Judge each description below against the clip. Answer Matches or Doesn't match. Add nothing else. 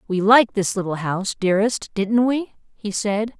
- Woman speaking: Matches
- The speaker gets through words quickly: Doesn't match